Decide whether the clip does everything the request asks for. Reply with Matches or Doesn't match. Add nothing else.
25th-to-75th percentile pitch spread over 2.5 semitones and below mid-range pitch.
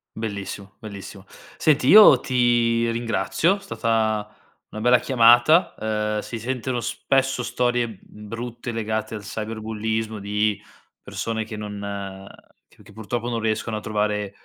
Doesn't match